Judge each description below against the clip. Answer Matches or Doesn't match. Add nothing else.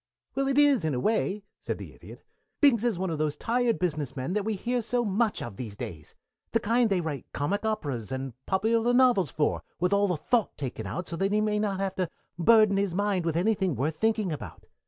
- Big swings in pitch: Matches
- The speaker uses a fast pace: Matches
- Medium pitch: Doesn't match